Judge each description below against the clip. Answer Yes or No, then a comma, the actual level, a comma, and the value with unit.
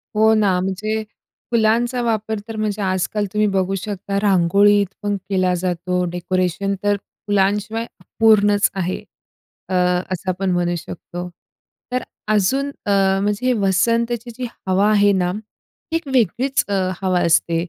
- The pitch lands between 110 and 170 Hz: No, high, 205 Hz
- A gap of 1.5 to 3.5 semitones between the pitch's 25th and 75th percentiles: Yes, average, 2.9 semitones